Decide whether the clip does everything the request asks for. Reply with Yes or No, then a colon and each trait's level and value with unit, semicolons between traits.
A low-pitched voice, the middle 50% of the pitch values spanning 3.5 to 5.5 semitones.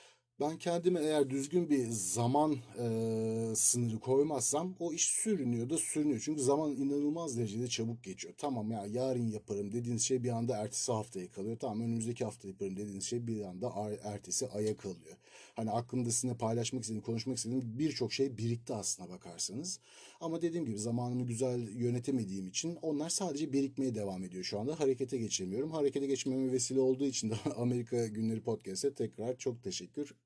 Yes: low, 120 Hz; average, 3.9 semitones